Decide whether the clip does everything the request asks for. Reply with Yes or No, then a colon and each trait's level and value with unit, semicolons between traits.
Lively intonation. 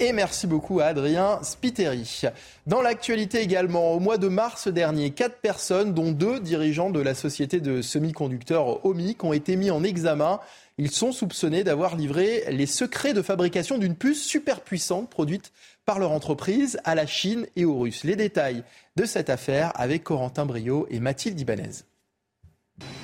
Yes: wide, 5.8 semitones